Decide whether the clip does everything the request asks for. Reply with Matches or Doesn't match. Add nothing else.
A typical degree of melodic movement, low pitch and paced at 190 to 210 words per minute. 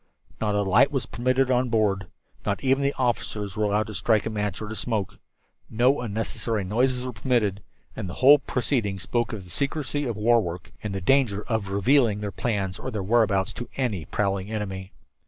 Matches